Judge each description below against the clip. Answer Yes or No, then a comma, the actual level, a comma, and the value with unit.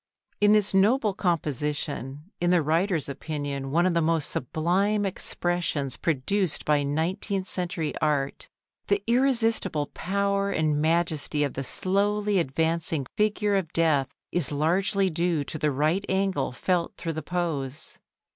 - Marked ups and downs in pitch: No, average, 4.7 semitones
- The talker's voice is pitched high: No, medium, 170 Hz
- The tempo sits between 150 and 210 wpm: No, slow, 135 wpm